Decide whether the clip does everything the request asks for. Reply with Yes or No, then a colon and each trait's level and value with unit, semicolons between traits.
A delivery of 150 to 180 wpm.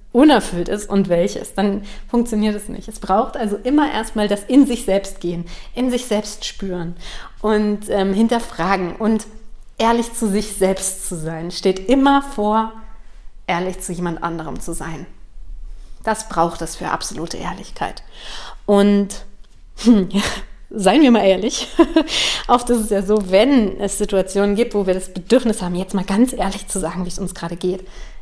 Yes: average, 170 wpm